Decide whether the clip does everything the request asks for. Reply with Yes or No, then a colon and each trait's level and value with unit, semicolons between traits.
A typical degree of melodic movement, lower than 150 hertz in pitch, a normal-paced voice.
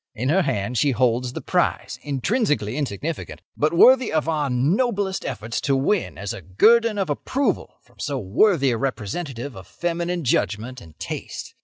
No: wide, 7.0 semitones; medium, 140 Hz; average, 165 wpm